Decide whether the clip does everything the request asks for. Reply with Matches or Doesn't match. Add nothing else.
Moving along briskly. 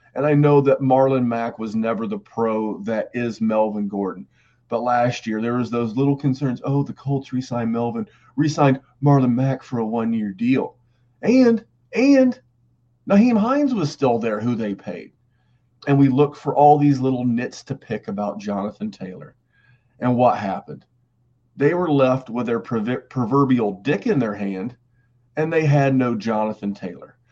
Doesn't match